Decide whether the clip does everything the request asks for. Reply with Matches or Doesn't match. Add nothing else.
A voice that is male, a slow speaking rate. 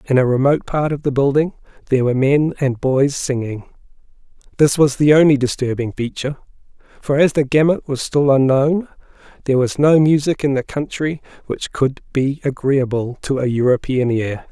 Doesn't match